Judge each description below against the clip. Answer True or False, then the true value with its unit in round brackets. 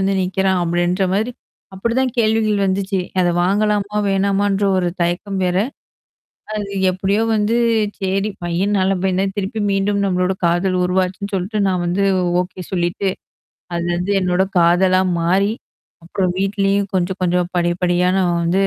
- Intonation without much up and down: True (1.8 semitones)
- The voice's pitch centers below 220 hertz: True (190 Hz)